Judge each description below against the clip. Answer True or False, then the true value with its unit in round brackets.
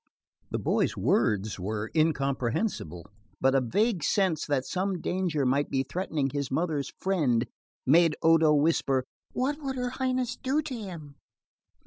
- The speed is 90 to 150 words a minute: True (140 wpm)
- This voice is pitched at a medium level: True (155 Hz)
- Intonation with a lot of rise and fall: True (6.4 semitones)